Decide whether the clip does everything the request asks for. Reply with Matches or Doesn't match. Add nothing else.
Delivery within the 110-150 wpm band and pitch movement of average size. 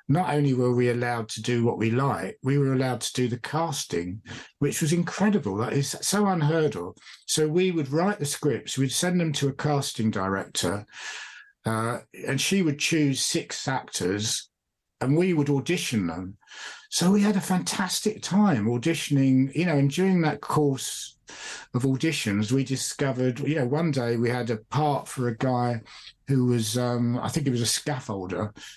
Doesn't match